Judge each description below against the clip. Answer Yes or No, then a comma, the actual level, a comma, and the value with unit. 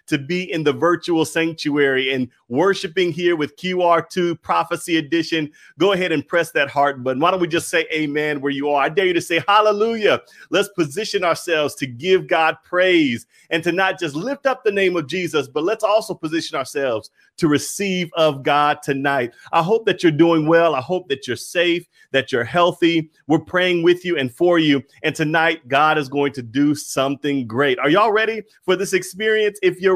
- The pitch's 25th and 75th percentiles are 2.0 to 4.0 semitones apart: Yes, average, 3.7 semitones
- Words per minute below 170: No, average, 200 wpm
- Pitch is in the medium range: Yes, medium, 165 Hz